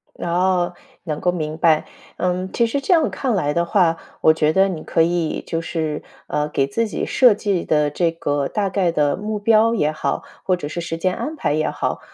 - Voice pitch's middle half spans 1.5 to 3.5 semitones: No, average, 4.1 semitones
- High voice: No, medium, 175 Hz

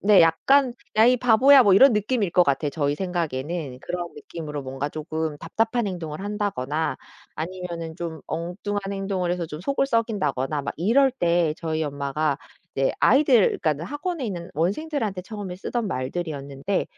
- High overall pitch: No, medium, 175 Hz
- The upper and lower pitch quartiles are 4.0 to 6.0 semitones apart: Yes, wide, 5.5 semitones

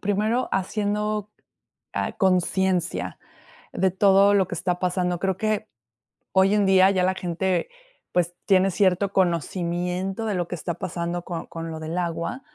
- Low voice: No, medium, 185 Hz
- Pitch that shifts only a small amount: Yes, narrow, 2.0 semitones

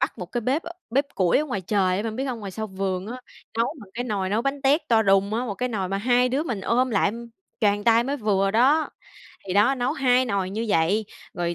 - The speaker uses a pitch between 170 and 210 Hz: No, high, 220 Hz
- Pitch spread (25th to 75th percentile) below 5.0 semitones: Yes, average, 4.3 semitones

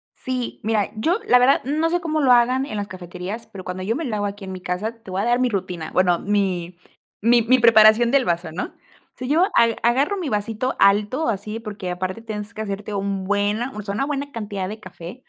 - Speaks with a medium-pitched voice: No, high, 215 Hz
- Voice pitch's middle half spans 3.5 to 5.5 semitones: Yes, average, 4.2 semitones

